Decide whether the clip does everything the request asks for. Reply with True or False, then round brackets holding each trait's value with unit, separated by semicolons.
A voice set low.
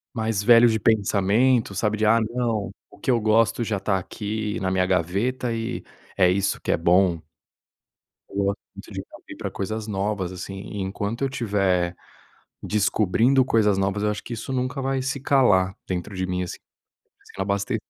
True (105 Hz)